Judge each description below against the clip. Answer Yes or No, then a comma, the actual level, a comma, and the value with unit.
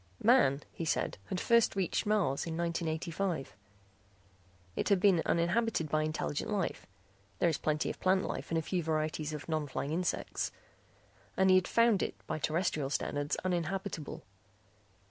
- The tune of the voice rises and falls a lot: No, average, 3.6 semitones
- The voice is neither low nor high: Yes, medium, 170 Hz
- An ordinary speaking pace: Yes, average, 155 wpm